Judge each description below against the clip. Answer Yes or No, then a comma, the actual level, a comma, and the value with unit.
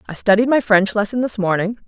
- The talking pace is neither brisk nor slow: No, fast, 225 wpm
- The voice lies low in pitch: No, high, 215 Hz